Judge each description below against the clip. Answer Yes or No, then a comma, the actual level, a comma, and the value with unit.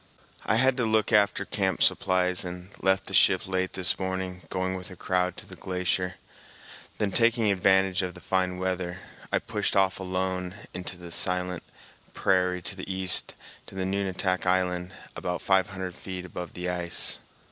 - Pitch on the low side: Yes, very low, 95 Hz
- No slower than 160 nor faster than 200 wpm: Yes, average, 170 wpm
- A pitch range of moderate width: No, narrow, 0.9 semitones